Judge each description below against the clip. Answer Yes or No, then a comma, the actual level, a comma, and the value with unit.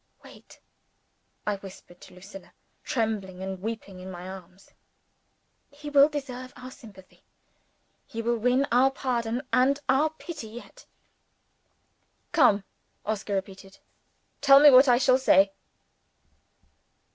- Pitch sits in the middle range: No, high, 230 Hz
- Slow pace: Yes, slow, 120 wpm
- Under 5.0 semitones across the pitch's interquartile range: No, wide, 5.4 semitones